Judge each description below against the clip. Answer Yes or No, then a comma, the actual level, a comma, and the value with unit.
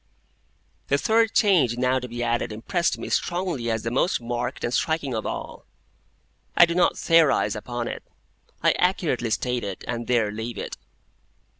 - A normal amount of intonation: No, wide, 6.0 semitones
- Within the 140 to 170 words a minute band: Yes, average, 165 wpm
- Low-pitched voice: Yes, low, 125 Hz